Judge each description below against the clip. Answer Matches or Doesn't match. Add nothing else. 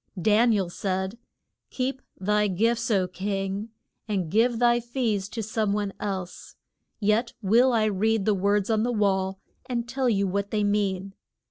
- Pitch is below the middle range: Doesn't match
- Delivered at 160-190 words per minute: Matches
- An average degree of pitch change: Matches